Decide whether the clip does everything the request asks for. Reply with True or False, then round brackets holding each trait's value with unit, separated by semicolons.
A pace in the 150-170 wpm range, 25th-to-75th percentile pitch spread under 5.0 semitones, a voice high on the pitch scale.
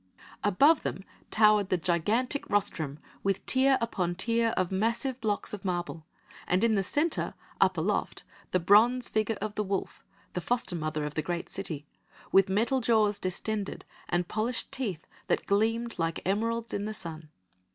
True (160 wpm; 4.5 semitones; 205 Hz)